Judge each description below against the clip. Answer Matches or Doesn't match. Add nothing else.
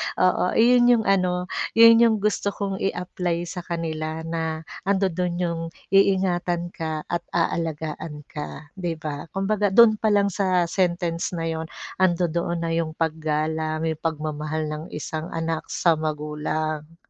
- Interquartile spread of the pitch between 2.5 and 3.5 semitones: Matches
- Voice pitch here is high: Doesn't match